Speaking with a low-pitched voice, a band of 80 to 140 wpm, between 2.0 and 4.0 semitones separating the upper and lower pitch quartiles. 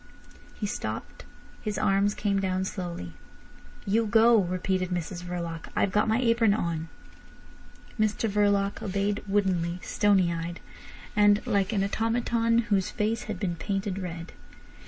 No: high, 200 Hz; slow, 135 wpm; average, 2.9 semitones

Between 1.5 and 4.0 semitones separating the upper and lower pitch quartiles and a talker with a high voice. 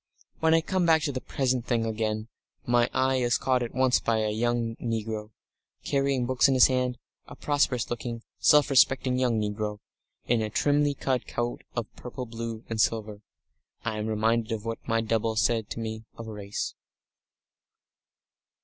No: average, 2.7 semitones; low, 115 Hz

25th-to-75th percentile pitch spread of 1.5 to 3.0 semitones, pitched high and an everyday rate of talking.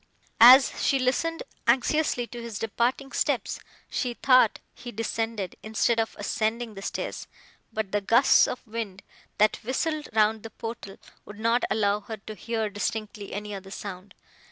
Yes: narrow, 2.6 semitones; high, 225 Hz; average, 155 wpm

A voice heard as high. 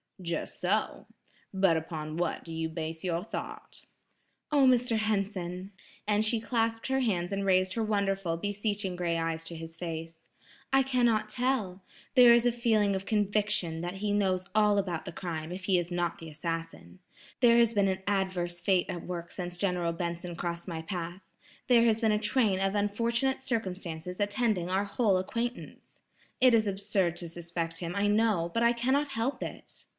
Yes: high, 195 Hz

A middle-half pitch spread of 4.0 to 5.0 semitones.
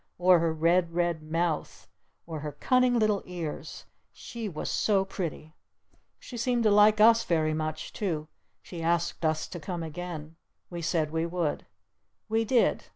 Yes: average, 4.7 semitones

